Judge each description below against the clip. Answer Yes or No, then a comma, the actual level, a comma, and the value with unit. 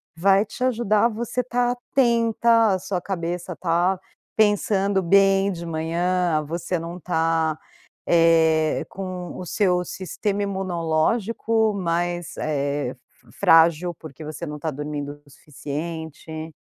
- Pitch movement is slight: No, average, 3.7 semitones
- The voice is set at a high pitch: No, medium, 175 Hz